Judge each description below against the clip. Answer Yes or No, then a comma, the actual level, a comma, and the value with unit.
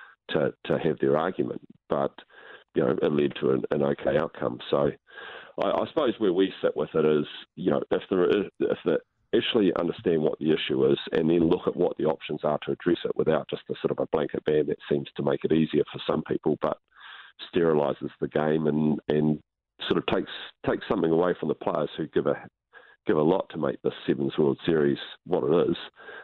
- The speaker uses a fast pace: Yes, fast, 215 wpm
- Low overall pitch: Yes, very low, 75 Hz